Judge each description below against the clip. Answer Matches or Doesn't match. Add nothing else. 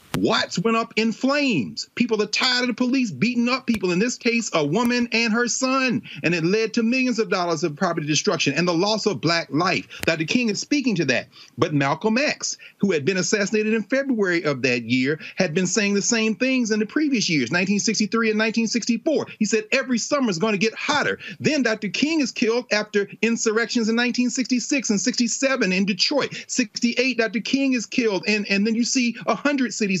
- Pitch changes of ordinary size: Matches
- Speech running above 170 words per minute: Matches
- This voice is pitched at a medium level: Doesn't match